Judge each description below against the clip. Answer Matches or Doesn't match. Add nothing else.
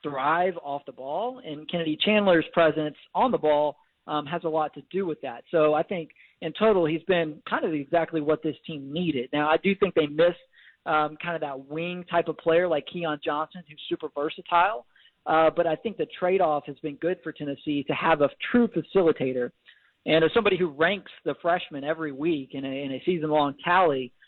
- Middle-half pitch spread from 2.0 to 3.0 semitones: Matches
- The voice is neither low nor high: Matches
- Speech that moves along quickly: Matches